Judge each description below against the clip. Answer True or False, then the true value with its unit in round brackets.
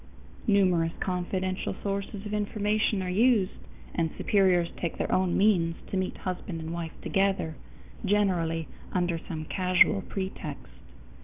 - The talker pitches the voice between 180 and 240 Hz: True (185 Hz)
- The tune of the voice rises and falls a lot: False (2.8 semitones)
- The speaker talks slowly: True (130 wpm)